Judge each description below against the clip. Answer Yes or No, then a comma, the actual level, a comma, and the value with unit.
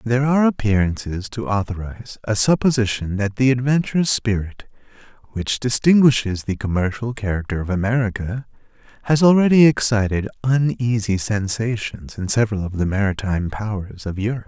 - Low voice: Yes, low, 110 Hz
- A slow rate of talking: Yes, slow, 130 wpm